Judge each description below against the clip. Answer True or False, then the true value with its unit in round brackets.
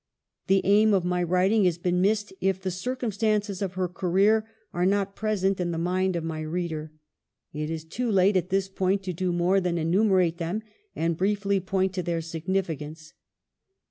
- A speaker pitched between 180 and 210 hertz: True (185 Hz)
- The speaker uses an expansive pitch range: False (2.5 semitones)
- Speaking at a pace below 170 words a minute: False (180 wpm)